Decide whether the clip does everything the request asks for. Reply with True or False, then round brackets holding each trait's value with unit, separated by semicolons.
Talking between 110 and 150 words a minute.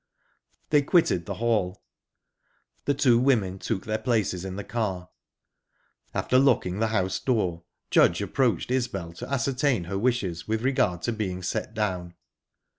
True (145 wpm)